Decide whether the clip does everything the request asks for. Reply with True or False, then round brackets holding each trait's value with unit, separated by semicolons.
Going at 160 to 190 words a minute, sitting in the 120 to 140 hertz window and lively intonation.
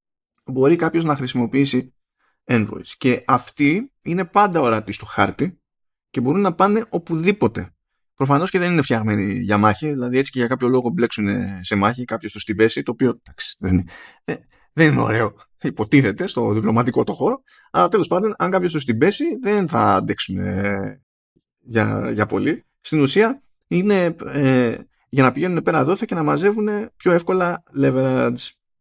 True (165 wpm; 135 Hz; 8.1 semitones)